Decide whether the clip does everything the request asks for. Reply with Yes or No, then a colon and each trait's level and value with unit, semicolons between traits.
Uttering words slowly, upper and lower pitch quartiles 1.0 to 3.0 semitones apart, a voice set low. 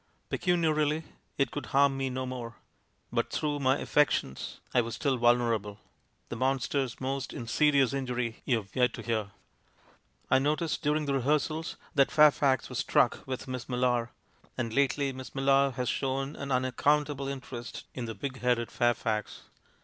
No: average, 155 wpm; average, 2.7 semitones; low, 130 Hz